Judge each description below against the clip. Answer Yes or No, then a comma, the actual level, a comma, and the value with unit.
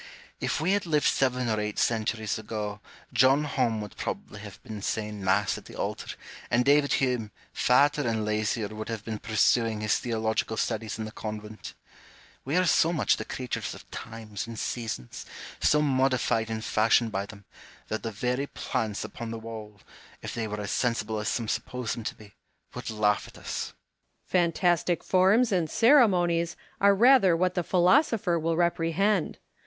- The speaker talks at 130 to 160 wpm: No, average, 175 wpm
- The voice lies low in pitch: Yes, low, 115 Hz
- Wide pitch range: Yes, wide, 7.3 semitones